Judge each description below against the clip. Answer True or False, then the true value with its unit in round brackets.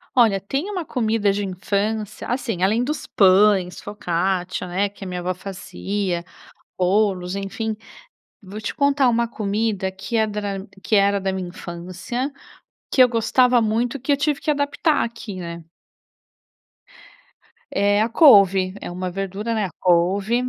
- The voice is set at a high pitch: True (205 Hz)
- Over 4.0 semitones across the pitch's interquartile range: False (3.7 semitones)